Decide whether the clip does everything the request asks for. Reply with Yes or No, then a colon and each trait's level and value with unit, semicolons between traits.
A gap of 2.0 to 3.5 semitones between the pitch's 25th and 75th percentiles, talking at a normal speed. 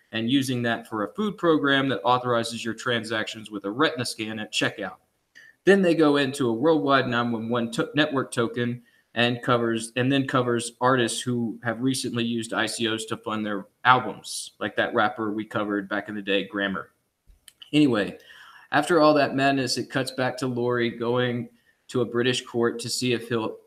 Yes: narrow, 2.6 semitones; average, 180 wpm